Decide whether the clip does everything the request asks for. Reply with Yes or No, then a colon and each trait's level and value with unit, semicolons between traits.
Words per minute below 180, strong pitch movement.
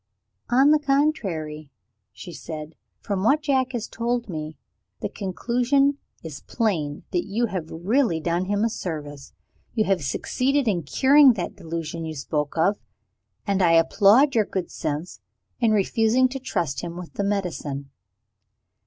Yes: average, 150 wpm; wide, 7.0 semitones